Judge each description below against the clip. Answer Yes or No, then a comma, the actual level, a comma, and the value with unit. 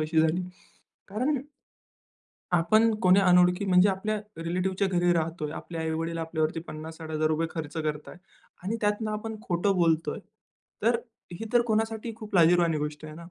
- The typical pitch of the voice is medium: Yes, medium, 175 Hz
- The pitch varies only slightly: No, average, 4.3 semitones